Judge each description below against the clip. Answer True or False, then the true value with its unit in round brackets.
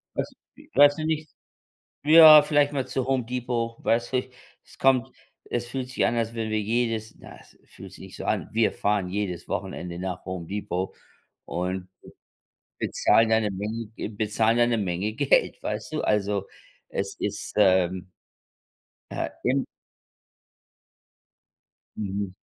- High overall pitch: False (110 Hz)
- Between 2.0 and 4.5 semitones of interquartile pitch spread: True (4.2 semitones)